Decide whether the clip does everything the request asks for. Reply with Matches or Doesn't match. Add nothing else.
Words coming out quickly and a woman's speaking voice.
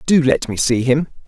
Doesn't match